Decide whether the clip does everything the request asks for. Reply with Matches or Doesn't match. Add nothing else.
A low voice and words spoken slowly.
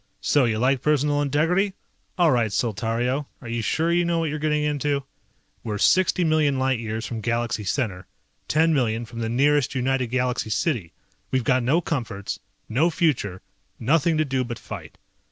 Doesn't match